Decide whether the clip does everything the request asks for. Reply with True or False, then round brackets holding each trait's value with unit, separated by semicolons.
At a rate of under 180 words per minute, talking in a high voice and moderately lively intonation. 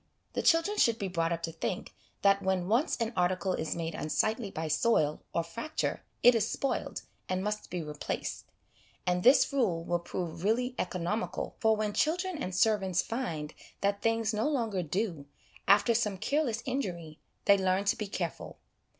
True (170 wpm; 200 Hz; 4.9 semitones)